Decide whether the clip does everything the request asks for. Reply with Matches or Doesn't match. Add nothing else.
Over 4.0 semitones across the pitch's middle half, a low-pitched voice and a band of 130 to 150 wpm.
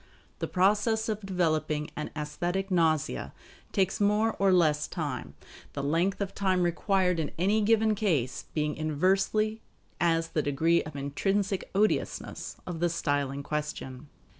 Doesn't match